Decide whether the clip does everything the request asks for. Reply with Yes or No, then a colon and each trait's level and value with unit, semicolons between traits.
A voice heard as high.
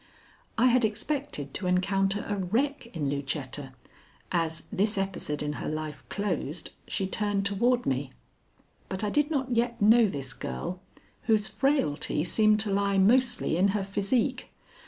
Yes: high, 200 Hz